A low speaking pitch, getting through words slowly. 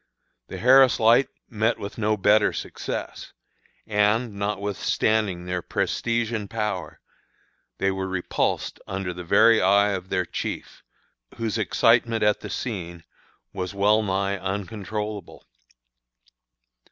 Yes: low, 105 Hz; slow, 115 wpm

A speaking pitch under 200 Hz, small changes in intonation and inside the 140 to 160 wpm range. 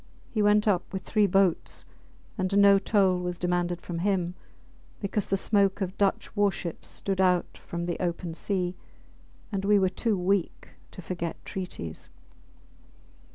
Yes: high, 190 Hz; narrow, 2.2 semitones; average, 155 wpm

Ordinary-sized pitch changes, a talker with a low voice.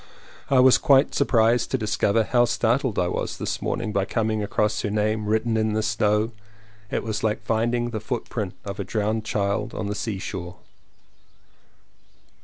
No: narrow, 1.9 semitones; low, 110 Hz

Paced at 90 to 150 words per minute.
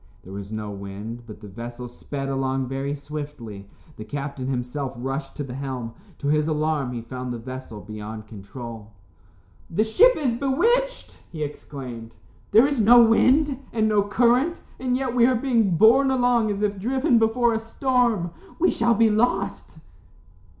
No: average, 165 wpm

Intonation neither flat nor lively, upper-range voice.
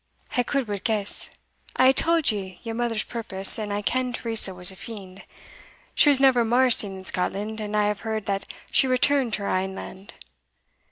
Yes: average, 3.8 semitones; high, 220 Hz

